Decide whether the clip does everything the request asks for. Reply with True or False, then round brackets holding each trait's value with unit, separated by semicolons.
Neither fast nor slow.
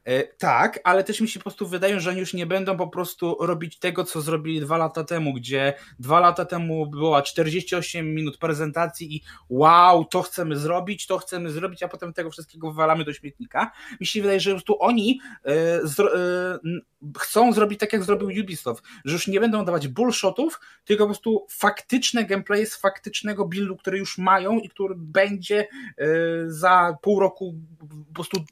False (175 wpm)